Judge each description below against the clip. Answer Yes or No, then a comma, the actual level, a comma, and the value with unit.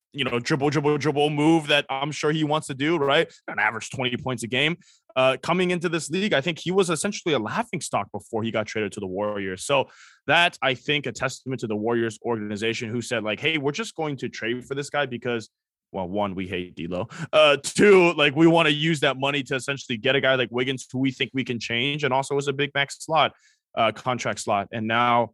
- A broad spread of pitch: No, average, 4.2 semitones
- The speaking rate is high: Yes, fast, 240 wpm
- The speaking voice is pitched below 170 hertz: Yes, low, 135 Hz